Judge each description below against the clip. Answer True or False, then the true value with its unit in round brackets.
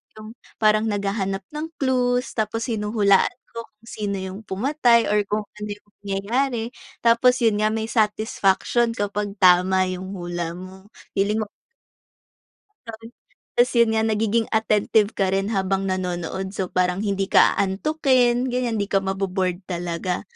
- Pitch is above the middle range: True (210 Hz)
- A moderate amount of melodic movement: True (3.0 semitones)